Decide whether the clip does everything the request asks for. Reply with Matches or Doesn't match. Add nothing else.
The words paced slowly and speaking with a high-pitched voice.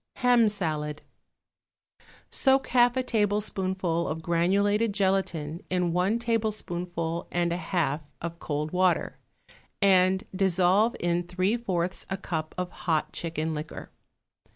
Doesn't match